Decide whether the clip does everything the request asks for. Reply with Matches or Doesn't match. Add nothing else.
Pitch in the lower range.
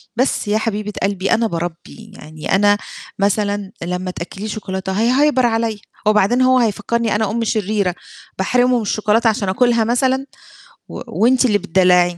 Doesn't match